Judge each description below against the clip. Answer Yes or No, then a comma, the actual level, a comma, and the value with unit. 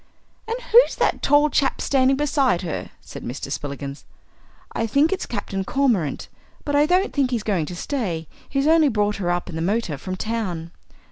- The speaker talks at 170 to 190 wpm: Yes, average, 185 wpm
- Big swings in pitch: Yes, wide, 8.3 semitones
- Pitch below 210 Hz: No, high, 225 Hz